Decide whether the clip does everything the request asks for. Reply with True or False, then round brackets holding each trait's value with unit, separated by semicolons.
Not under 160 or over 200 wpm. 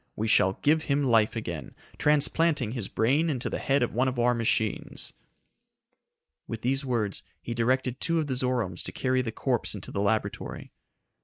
True (175 wpm)